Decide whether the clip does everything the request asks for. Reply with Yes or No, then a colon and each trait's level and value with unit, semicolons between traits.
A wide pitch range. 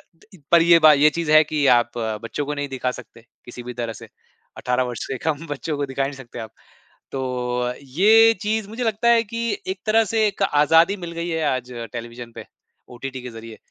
Yes: wide, 6.7 semitones